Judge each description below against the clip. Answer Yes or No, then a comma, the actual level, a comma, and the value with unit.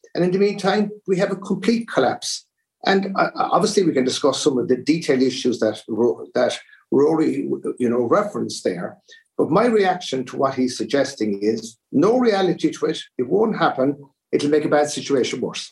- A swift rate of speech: No, average, 175 wpm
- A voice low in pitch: No, medium, 150 Hz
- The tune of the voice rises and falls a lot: Yes, wide, 7.6 semitones